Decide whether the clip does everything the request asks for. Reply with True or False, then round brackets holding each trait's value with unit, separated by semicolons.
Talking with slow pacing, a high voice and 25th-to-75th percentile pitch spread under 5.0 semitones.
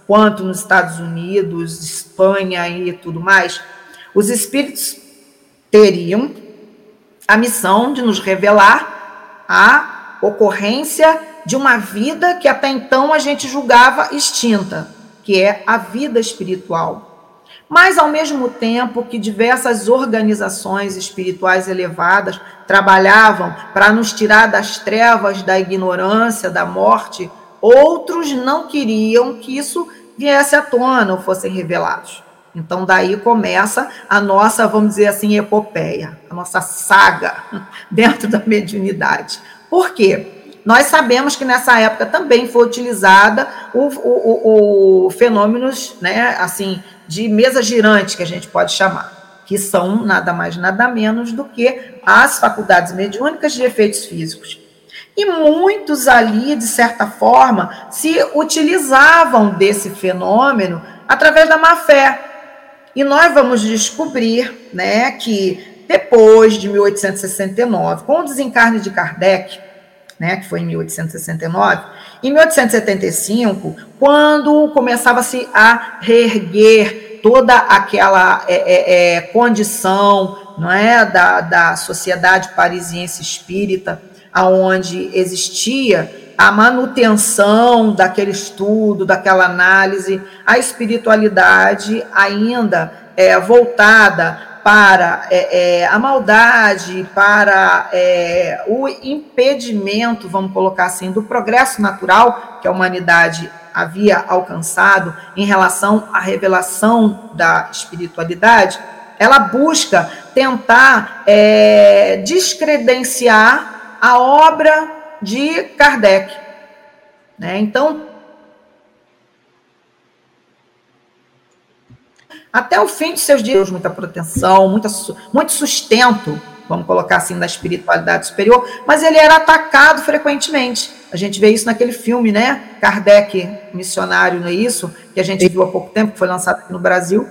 False (115 wpm; 215 Hz; 5.3 semitones)